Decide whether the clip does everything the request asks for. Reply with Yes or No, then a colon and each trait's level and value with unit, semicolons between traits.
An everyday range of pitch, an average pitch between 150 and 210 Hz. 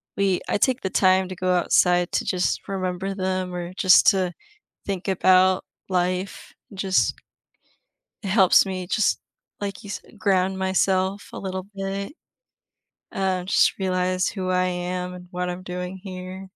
No: narrow, 1.0 semitones; medium, 185 Hz